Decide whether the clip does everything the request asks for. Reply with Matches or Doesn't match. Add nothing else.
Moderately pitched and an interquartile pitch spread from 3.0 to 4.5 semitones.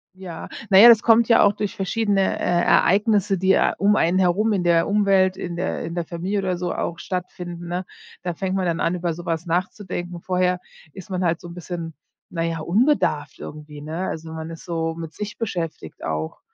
Doesn't match